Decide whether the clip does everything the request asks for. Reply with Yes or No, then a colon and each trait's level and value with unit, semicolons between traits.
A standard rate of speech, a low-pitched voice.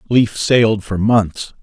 Yes: average, 150 wpm; low, 105 Hz